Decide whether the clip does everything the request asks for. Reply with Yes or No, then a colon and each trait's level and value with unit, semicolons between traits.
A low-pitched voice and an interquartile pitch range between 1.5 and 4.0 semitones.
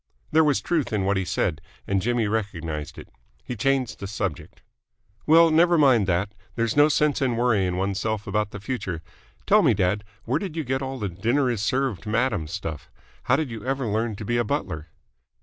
No: low, 110 Hz; wide, 5.4 semitones